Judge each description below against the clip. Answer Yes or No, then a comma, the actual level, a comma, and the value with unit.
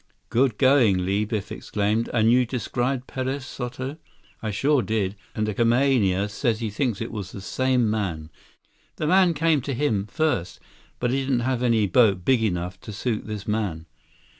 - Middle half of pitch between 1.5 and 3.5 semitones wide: No, average, 4.2 semitones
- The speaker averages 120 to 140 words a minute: No, average, 175 wpm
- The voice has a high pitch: No, low, 115 Hz